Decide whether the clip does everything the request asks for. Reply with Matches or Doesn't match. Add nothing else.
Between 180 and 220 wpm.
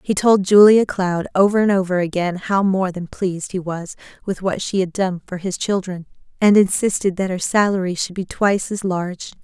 Matches